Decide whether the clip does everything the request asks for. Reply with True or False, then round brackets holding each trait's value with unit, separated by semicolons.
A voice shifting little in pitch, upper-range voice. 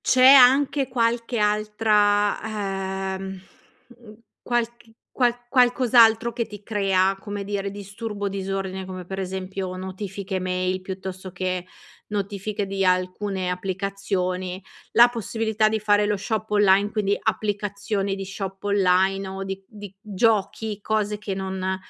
True (2.1 semitones; 200 Hz)